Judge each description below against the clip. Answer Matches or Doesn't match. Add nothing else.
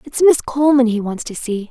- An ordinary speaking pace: Doesn't match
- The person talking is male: Doesn't match